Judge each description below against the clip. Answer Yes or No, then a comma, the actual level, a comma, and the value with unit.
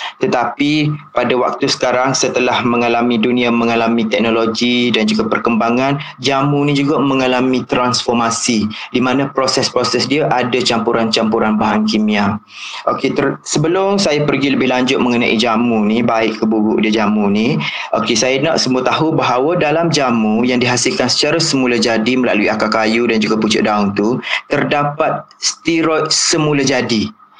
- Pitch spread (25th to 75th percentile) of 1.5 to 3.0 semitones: No, average, 3.5 semitones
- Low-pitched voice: Yes, low, 125 Hz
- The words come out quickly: No, average, 145 wpm